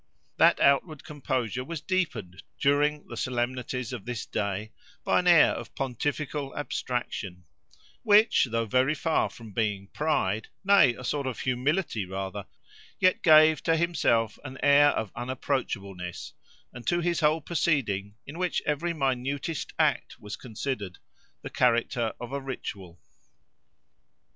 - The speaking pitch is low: Yes, low, 130 Hz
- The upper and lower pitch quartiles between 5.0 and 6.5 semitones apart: Yes, wide, 5.4 semitones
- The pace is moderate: No, slow, 130 wpm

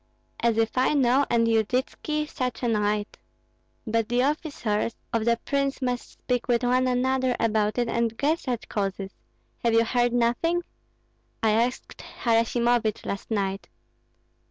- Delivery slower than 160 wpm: Yes, average, 145 wpm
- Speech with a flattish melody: Yes, narrow, 2.2 semitones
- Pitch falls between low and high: No, high, 235 Hz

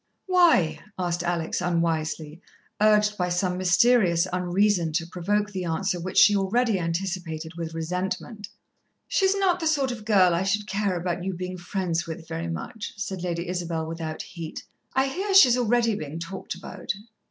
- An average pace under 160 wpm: No, average, 165 wpm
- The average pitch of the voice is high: No, medium, 180 Hz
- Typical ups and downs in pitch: Yes, average, 3.7 semitones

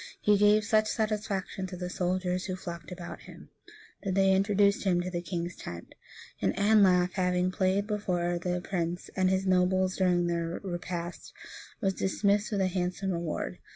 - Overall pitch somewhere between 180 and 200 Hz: Yes, medium, 185 Hz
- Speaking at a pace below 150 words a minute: No, average, 165 wpm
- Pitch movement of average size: No, narrow, 2.0 semitones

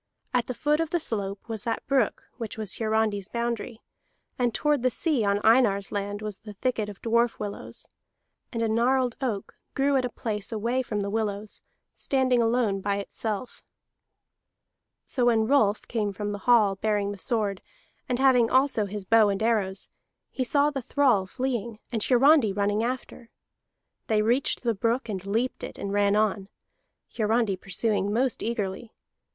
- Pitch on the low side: No, high, 225 Hz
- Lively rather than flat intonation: No, average, 3.4 semitones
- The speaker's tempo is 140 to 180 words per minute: Yes, average, 170 wpm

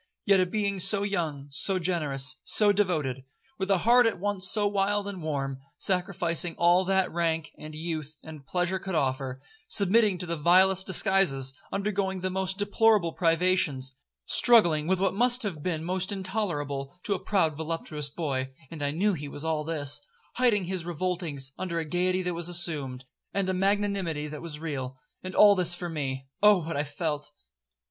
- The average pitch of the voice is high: No, medium, 175 Hz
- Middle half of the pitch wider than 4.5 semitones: No, average, 4.2 semitones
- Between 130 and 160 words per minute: No, average, 170 wpm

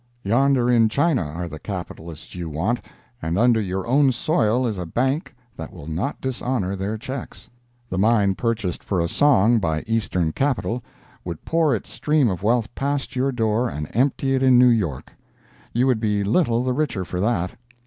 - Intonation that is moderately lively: No, wide, 5.8 semitones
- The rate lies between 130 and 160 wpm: No, average, 180 wpm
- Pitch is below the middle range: Yes, low, 115 Hz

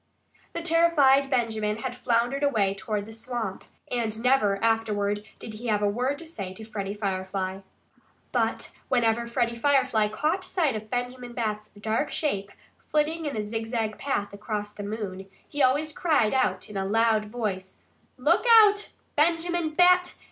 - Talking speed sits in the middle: Yes, average, 155 wpm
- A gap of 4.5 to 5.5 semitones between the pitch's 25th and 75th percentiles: Yes, average, 4.9 semitones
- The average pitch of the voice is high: Yes, high, 230 Hz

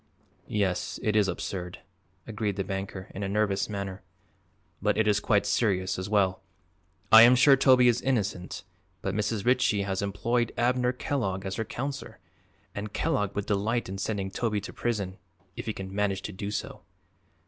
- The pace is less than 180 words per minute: Yes, average, 170 wpm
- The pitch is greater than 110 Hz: No, low, 105 Hz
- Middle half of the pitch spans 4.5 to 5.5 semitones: No, average, 3.0 semitones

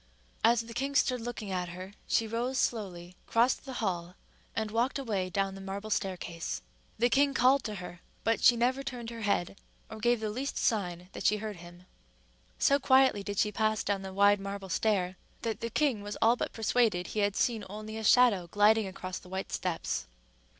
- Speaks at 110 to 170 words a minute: No, average, 200 wpm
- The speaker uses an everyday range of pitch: Yes, average, 3.7 semitones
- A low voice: No, high, 210 Hz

